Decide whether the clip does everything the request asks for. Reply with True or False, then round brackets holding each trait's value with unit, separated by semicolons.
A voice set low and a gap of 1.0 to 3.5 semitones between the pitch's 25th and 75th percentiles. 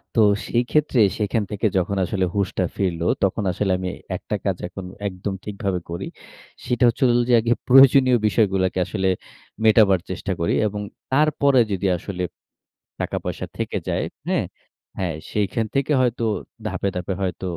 False (100 Hz; 4.3 semitones)